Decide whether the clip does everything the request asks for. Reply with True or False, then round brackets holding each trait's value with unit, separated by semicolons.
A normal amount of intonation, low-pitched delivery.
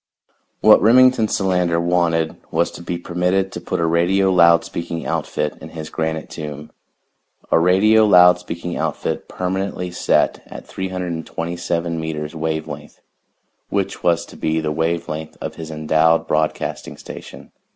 False (2.1 semitones; 85 Hz)